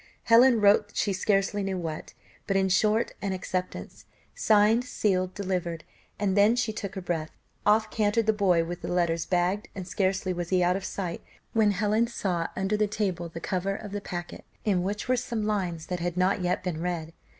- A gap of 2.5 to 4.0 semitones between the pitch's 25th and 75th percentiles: Yes, average, 2.8 semitones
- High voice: Yes, high, 195 Hz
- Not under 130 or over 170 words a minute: No, average, 195 wpm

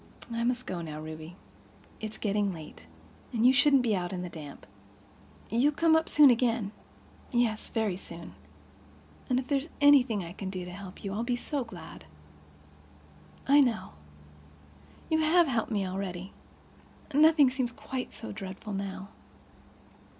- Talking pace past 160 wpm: No, average, 150 wpm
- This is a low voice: No, high, 220 Hz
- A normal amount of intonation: No, wide, 5.9 semitones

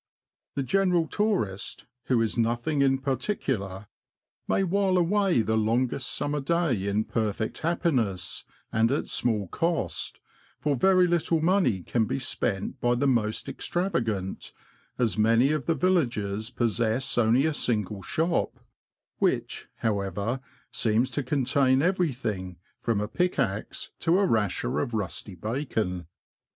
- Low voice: Yes, low, 120 Hz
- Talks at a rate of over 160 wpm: No, slow, 135 wpm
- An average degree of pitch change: No, wide, 6.8 semitones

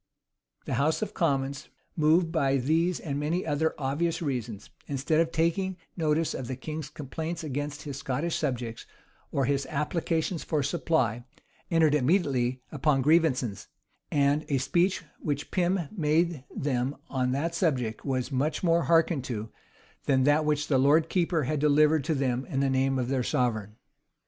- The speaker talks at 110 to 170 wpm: Yes, average, 160 wpm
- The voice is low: No, medium, 145 Hz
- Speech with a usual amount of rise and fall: Yes, average, 3.5 semitones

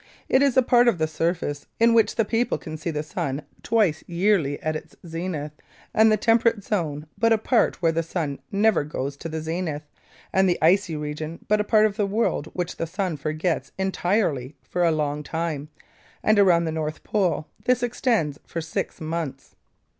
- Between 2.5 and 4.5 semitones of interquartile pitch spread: No, wide, 5.4 semitones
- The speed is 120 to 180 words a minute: No, average, 190 wpm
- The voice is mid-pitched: Yes, medium, 170 Hz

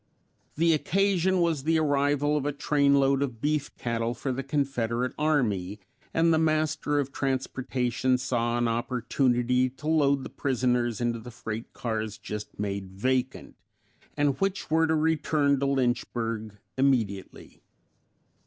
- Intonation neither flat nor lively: Yes, average, 3.8 semitones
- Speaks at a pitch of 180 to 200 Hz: No, low, 130 Hz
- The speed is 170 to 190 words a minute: No, slow, 135 wpm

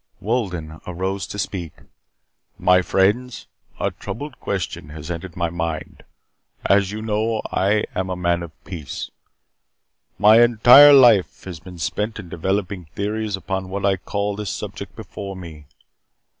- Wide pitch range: No, average, 3.4 semitones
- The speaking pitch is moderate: No, very low, 95 Hz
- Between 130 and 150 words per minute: Yes, average, 145 wpm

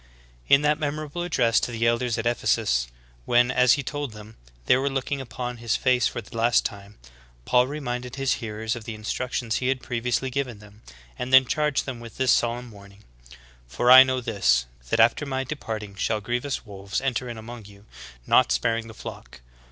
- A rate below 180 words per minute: No, average, 200 wpm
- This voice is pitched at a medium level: No, low, 120 Hz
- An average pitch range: Yes, average, 3.1 semitones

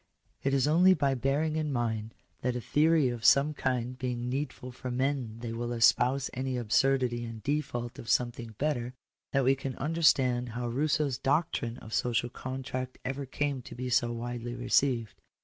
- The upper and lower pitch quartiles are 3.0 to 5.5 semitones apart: No, narrow, 2.4 semitones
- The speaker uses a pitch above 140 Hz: No, low, 125 Hz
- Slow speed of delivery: No, average, 180 wpm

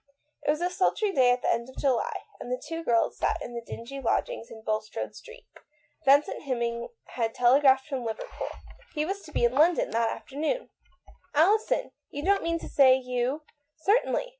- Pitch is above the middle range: Yes, very high, 275 Hz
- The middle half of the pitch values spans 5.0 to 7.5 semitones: Yes, average, 5.3 semitones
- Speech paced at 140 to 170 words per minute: No, fast, 205 wpm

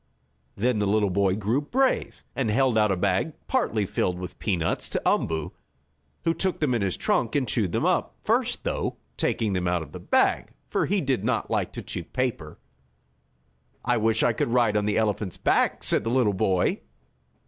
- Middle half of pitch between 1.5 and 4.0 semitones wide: No, average, 5.0 semitones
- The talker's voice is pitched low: Yes, low, 105 Hz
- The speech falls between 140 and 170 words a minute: No, average, 190 wpm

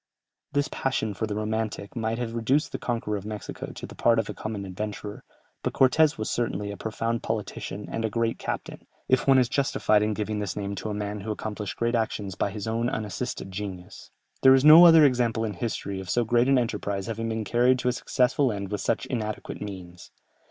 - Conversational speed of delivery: No, fast, 215 wpm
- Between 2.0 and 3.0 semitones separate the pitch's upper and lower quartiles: Yes, average, 2.7 semitones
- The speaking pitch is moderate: No, low, 110 Hz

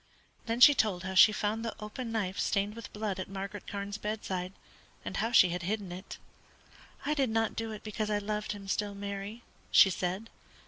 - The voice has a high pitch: Yes, high, 210 Hz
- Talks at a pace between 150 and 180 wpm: No, average, 195 wpm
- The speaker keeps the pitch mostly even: Yes, narrow, 2.1 semitones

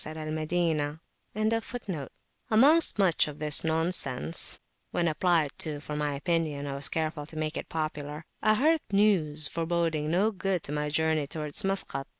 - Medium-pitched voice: Yes, medium, 160 Hz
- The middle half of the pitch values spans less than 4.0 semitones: Yes, average, 3.4 semitones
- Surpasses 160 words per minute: No, average, 150 wpm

